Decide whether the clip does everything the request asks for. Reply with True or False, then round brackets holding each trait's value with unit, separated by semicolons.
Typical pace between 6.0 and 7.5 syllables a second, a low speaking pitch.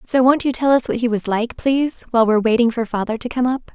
False (6.5 syllables/s; 240 Hz)